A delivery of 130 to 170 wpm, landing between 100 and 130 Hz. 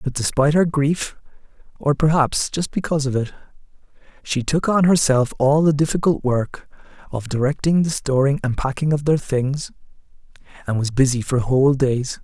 No: average, 160 wpm; medium, 140 Hz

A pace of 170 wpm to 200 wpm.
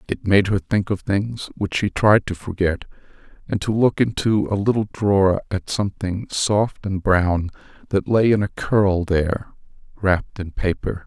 Yes: average, 175 wpm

